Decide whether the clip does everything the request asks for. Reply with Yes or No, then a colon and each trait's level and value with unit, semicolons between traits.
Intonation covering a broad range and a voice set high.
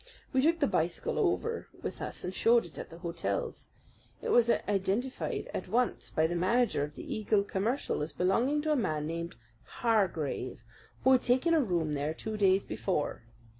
Yes: wide, 6.8 semitones; high, 200 Hz